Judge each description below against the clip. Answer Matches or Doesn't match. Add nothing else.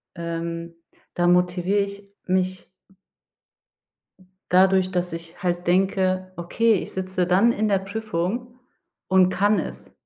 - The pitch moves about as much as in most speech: Doesn't match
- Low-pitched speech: Doesn't match